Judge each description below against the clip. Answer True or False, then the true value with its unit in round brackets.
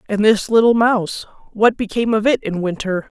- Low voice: False (215 Hz)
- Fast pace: False (190 wpm)